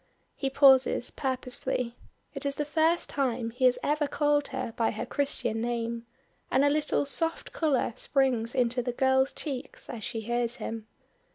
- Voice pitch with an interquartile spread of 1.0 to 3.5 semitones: Yes, average, 3.2 semitones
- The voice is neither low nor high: No, very high, 260 Hz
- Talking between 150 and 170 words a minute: Yes, average, 165 wpm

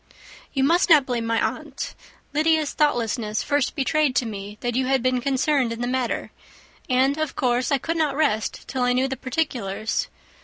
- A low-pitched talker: No, very high, 260 Hz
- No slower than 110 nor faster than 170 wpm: No, average, 185 wpm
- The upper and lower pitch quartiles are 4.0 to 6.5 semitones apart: No, average, 3.5 semitones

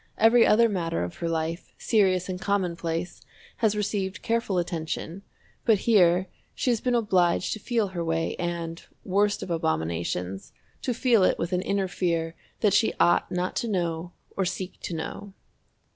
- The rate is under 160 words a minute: No, average, 165 wpm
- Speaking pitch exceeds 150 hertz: Yes, medium, 185 Hz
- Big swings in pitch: No, average, 3.6 semitones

